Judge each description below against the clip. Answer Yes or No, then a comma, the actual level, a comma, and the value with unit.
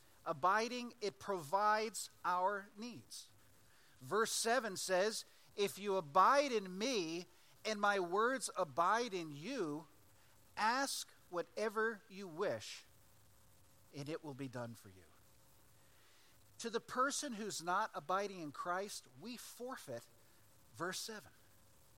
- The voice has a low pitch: No, medium, 185 Hz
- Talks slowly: Yes, slow, 115 wpm